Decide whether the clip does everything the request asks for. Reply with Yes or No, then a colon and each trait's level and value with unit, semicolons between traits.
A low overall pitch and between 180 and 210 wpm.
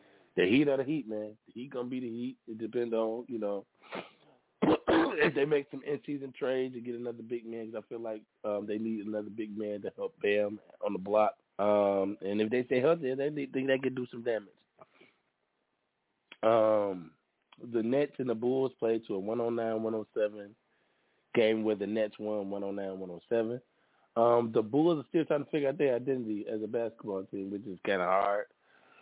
Yes: low, 115 Hz; average, 195 wpm